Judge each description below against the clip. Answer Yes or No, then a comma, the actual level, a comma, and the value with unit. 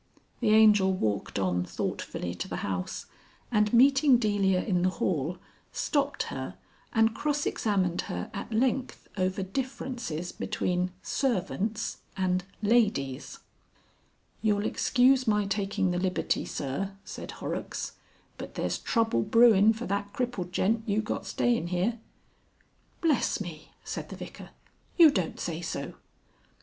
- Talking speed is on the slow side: Yes, slow, 130 wpm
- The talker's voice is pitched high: Yes, high, 205 Hz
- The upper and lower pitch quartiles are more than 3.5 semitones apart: Yes, average, 4.5 semitones